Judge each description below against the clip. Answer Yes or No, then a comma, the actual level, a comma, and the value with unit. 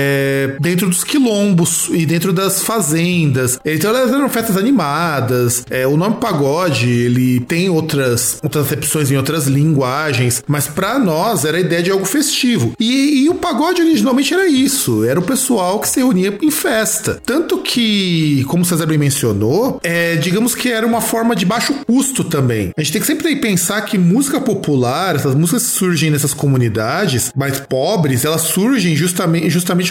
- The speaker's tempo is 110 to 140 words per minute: No, average, 175 wpm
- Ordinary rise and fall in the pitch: No, wide, 8.1 semitones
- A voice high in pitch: No, medium, 175 Hz